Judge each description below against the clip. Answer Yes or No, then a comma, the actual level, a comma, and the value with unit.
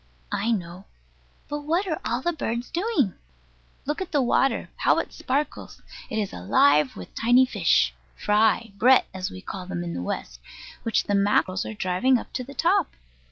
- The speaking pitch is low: No, high, 225 Hz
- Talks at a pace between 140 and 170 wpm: No, average, 180 wpm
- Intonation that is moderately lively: No, wide, 6.9 semitones